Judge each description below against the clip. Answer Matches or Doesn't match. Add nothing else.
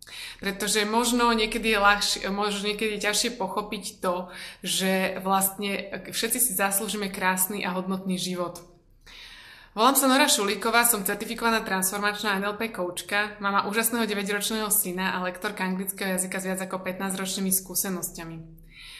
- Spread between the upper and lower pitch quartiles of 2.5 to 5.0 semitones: Doesn't match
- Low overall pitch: Doesn't match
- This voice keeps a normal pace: Matches